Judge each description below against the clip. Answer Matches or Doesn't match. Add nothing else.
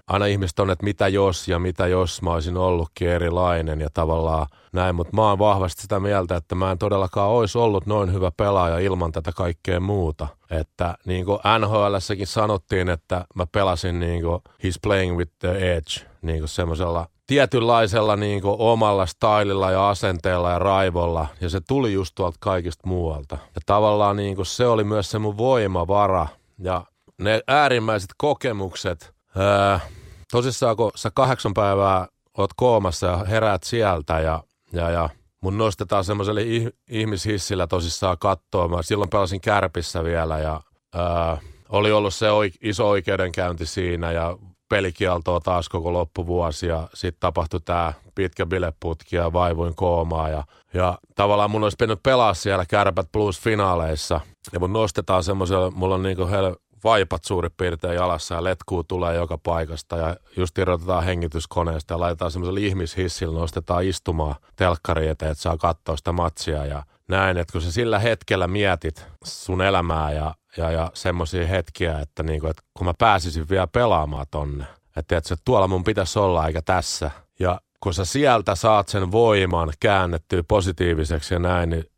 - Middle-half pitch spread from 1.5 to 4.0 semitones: Matches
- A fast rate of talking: Matches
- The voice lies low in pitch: Matches